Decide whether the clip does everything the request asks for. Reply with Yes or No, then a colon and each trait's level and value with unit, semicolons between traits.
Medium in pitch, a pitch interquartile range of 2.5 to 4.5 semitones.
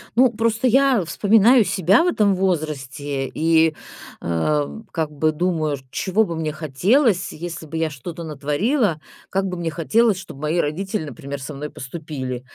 No: medium, 165 Hz; average, 5.0 semitones